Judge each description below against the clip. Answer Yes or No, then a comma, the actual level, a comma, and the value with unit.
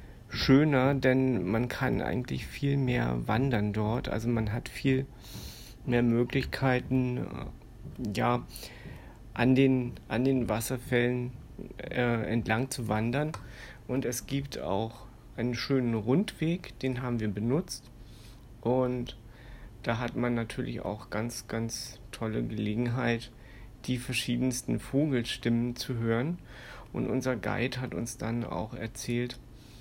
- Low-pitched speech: Yes, low, 120 Hz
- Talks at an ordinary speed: No, slow, 120 wpm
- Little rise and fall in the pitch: Yes, narrow, 2.1 semitones